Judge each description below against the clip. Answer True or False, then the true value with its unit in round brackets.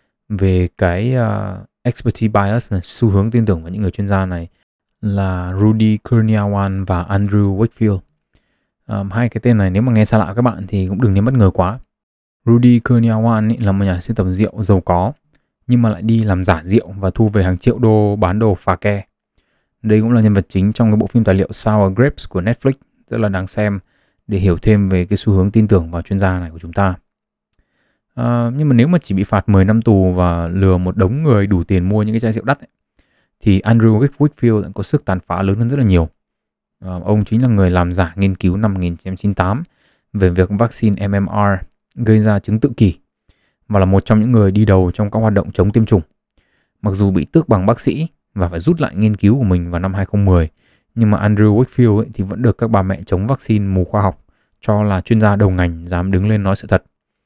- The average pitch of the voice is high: False (100 Hz)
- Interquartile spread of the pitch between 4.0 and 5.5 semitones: False (3.1 semitones)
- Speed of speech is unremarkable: True (230 wpm)